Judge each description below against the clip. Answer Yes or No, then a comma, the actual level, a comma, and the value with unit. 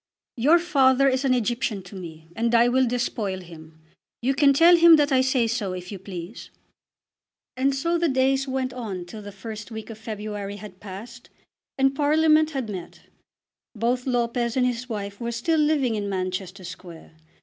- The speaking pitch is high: Yes, high, 235 Hz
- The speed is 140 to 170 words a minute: No, average, 180 wpm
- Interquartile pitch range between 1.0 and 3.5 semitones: No, average, 4.9 semitones